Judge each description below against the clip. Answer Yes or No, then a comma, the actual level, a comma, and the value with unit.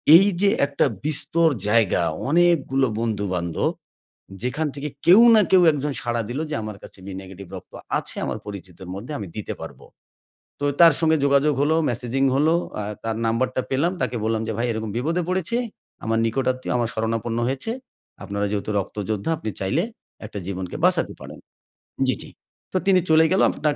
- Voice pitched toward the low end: Yes, low, 125 Hz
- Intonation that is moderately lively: No, wide, 6.2 semitones